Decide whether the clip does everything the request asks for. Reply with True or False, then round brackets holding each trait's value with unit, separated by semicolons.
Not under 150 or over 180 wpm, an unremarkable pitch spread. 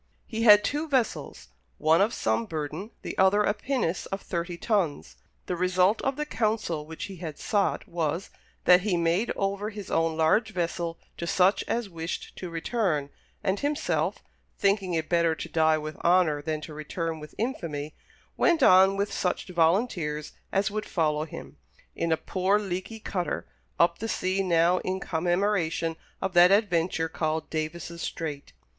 True (165 wpm; 3.8 semitones)